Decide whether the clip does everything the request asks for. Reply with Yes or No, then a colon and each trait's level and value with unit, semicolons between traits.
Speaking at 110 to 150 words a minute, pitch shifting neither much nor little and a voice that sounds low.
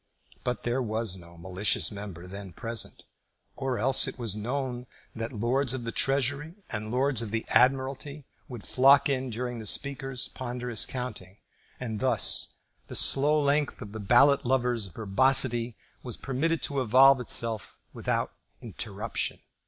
Yes: average, 145 wpm; average, 3.5 semitones; low, 125 Hz